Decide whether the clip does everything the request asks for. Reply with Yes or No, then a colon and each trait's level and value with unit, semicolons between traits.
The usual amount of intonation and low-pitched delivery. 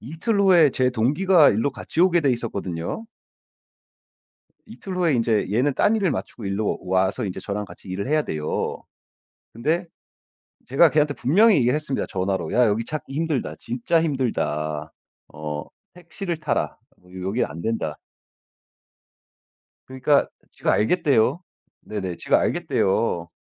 No: wide, 8.0 semitones; low, 125 Hz